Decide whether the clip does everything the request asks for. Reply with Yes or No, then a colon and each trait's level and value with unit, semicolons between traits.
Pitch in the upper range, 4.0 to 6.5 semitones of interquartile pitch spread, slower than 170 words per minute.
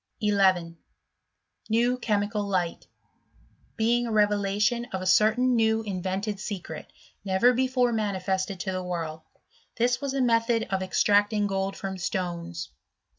No: high, 205 Hz; average, 3.4 semitones; slow, 135 wpm